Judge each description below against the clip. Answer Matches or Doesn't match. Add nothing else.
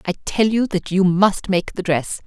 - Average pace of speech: Doesn't match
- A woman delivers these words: Matches